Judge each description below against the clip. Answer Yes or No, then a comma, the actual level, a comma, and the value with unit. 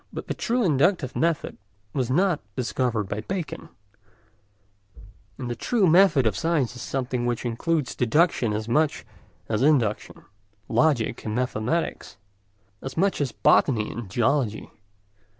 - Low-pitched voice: Yes, low, 130 Hz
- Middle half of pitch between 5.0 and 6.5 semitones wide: Yes, wide, 5.6 semitones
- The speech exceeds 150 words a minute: No, slow, 135 wpm